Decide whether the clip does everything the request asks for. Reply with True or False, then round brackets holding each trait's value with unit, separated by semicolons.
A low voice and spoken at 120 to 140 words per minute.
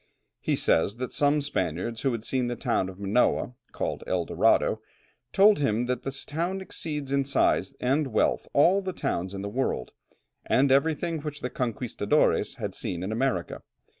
False (130 Hz; 170 wpm)